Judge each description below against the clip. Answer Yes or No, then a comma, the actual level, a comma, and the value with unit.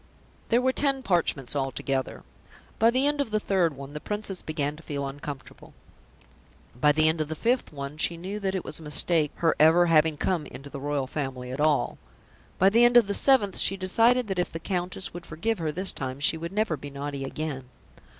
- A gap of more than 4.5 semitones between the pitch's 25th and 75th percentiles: Yes, wide, 5.4 semitones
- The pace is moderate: No, fast, 215 wpm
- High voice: No, medium, 160 Hz